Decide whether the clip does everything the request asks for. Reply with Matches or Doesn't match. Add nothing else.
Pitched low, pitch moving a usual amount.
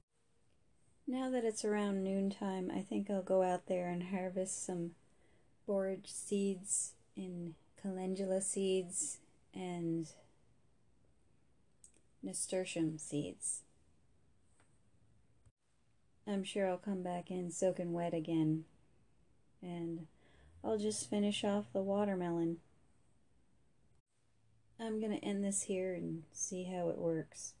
Doesn't match